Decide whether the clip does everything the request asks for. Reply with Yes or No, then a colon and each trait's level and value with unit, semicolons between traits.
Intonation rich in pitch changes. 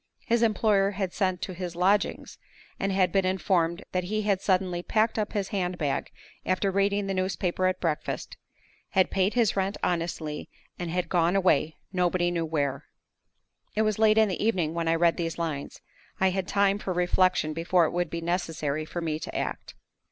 No: narrow, 2.6 semitones